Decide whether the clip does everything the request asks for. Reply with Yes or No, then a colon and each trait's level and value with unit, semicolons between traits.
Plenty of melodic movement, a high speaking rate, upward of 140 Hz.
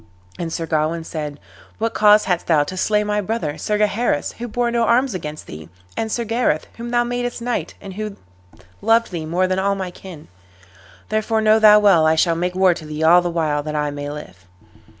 Yes: wide, 5.7 semitones; fast, 210 wpm; medium, 185 Hz